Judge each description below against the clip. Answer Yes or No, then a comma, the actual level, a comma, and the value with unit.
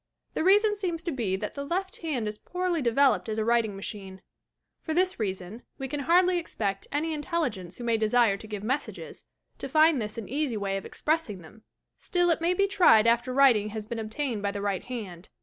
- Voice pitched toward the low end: No, high, 240 Hz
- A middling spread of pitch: No, wide, 7.4 semitones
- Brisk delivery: Yes, fast, 215 wpm